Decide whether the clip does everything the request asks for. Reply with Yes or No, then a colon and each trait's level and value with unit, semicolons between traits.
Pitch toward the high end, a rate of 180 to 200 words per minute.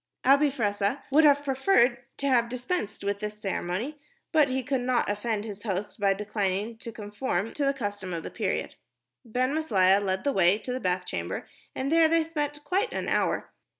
Yes: high, 235 Hz; average, 190 wpm